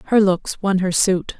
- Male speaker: No, female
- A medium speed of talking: No, fast, 215 wpm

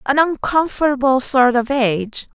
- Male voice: No, female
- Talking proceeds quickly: No, slow, 125 wpm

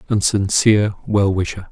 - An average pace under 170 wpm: Yes, average, 140 wpm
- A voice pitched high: No, low, 100 Hz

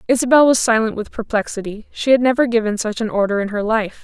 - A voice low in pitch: No, high, 225 Hz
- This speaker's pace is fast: Yes, fast, 225 wpm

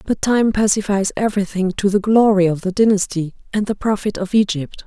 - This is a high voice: Yes, high, 200 Hz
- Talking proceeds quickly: No, average, 185 wpm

